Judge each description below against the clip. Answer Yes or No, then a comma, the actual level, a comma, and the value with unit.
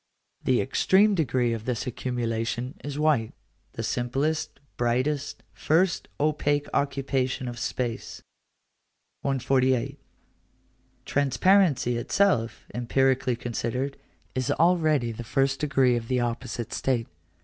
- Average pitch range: Yes, average, 3.2 semitones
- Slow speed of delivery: Yes, slow, 105 wpm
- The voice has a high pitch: No, low, 130 Hz